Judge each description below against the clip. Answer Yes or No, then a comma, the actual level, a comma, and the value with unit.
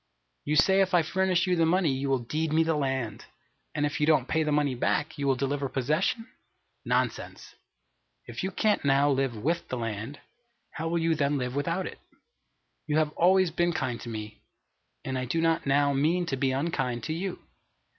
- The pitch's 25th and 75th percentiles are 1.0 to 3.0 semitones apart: No, average, 3.8 semitones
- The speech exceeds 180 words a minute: Yes, average, 200 wpm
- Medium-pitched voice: Yes, medium, 150 Hz